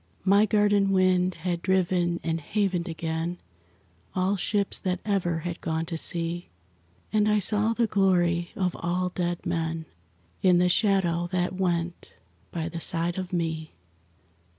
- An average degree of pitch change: No, narrow, 2.1 semitones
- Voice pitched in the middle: Yes, medium, 180 Hz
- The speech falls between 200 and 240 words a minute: No, average, 145 wpm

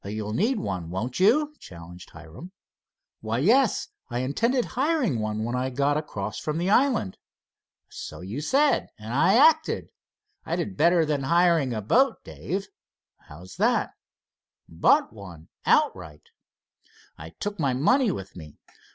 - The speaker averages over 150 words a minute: No, average, 145 wpm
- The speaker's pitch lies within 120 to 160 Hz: Yes, medium, 140 Hz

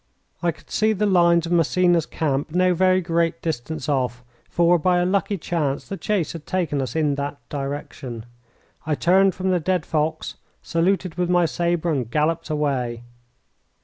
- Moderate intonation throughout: Yes, average, 3.3 semitones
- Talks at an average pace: Yes, average, 170 wpm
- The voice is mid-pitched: Yes, medium, 165 Hz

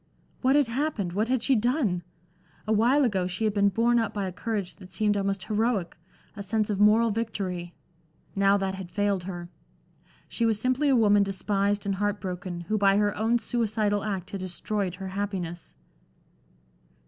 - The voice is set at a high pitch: Yes, high, 205 Hz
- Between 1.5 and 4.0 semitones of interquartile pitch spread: Yes, average, 2.8 semitones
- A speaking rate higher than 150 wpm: Yes, average, 175 wpm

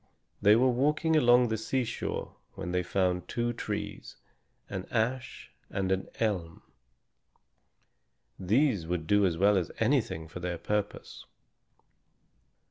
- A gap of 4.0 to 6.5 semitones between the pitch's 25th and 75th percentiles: Yes, average, 5.1 semitones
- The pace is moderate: No, slow, 125 wpm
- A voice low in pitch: Yes, low, 100 Hz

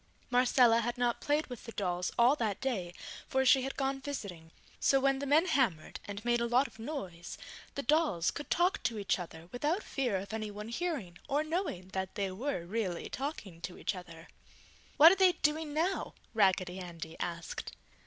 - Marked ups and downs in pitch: Yes, wide, 7.3 semitones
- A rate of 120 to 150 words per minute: No, average, 185 wpm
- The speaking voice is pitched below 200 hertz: No, high, 235 Hz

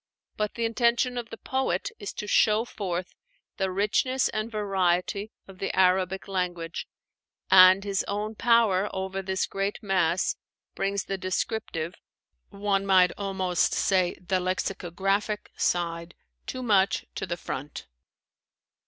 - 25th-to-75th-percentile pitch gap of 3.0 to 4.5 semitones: No, narrow, 2.4 semitones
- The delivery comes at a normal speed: No, slow, 130 wpm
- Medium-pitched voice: No, high, 195 Hz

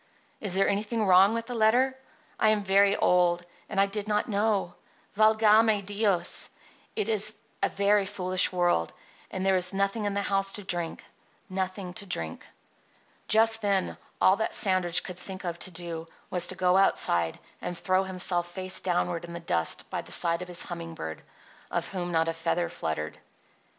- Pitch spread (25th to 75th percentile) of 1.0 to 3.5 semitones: Yes, average, 2.8 semitones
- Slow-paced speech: No, average, 180 wpm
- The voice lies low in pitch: No, high, 190 Hz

